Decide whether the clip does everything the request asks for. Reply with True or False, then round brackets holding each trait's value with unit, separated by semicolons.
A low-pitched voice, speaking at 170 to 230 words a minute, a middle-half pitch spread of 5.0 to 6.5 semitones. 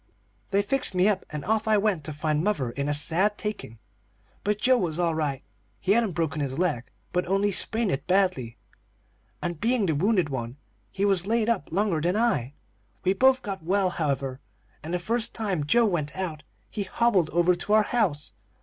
False (185 Hz; 195 wpm; 5.5 semitones)